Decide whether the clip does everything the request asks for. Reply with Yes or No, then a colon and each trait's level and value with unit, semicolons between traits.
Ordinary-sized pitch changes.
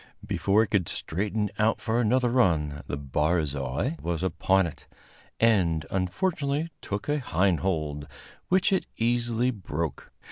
No: wide, 6.8 semitones